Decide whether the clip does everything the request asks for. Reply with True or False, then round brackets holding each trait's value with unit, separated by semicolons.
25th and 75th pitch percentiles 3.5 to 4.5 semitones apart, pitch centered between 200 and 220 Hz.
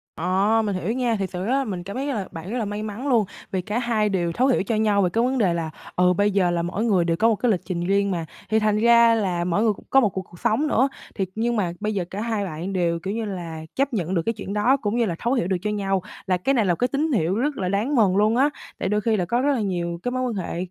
True (4.1 semitones; 205 Hz)